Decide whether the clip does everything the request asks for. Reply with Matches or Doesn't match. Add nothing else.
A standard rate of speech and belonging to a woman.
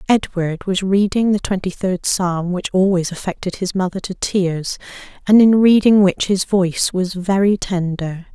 Matches